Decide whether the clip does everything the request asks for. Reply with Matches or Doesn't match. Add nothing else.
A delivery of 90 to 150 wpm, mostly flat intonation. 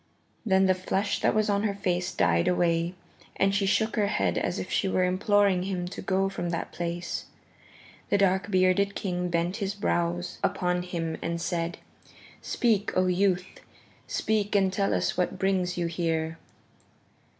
Doesn't match